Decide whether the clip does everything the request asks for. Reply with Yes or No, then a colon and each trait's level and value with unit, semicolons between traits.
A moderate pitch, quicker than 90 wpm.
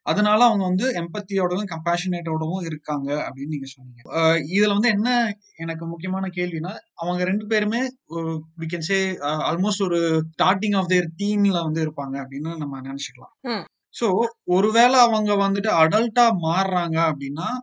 Yes: medium, 180 Hz; average, 125 wpm